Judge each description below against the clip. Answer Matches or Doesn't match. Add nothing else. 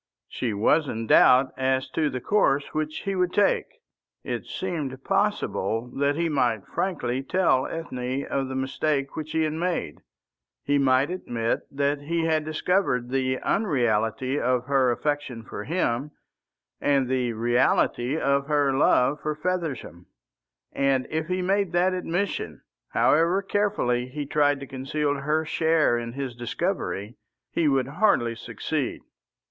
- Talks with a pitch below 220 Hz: Matches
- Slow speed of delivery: Doesn't match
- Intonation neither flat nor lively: Matches